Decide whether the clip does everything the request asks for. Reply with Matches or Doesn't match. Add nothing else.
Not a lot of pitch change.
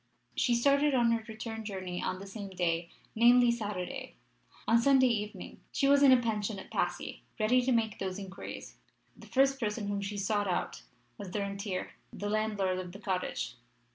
Doesn't match